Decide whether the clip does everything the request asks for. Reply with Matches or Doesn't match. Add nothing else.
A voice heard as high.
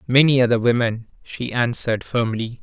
Doesn't match